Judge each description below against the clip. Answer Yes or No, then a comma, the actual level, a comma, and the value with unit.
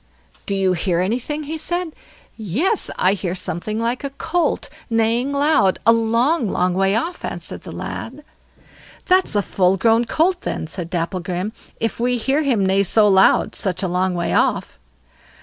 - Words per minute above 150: Yes, average, 165 wpm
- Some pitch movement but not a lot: No, wide, 6.9 semitones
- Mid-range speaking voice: No, high, 220 Hz